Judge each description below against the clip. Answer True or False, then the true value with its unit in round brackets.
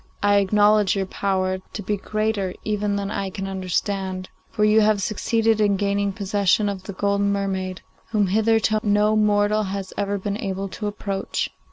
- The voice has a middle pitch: False (200 Hz)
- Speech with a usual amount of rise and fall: False (1.5 semitones)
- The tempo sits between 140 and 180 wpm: True (170 wpm)